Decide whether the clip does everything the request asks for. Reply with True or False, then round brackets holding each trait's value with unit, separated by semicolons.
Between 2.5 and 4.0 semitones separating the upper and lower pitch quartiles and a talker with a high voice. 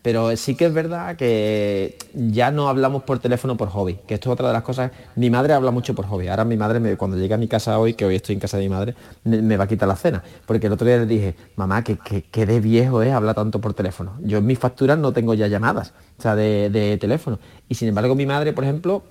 False (3.4 semitones; 115 Hz)